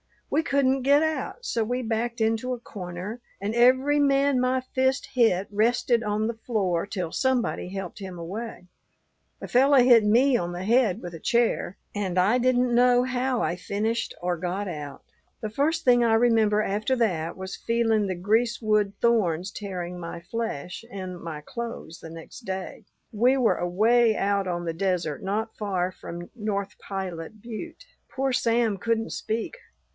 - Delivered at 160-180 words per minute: Yes, average, 165 wpm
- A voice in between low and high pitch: No, high, 220 Hz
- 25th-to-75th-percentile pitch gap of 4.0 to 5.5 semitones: Yes, average, 4.7 semitones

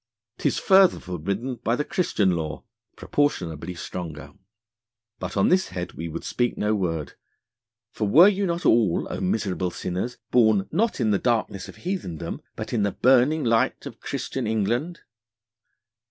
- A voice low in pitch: Yes, low, 110 Hz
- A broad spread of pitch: Yes, wide, 6.9 semitones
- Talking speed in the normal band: Yes, average, 155 wpm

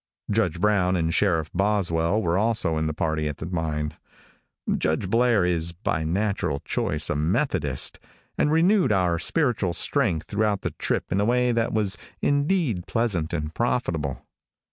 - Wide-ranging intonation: Yes, wide, 5.7 semitones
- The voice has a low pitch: Yes, very low, 90 Hz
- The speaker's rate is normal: Yes, average, 155 wpm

